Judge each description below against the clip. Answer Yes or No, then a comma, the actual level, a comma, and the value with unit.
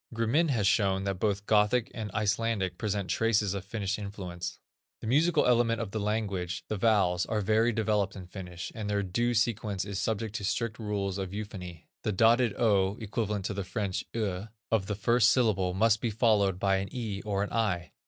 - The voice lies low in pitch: Yes, low, 105 Hz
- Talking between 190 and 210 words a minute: Yes, average, 195 wpm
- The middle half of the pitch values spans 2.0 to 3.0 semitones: Yes, narrow, 2.6 semitones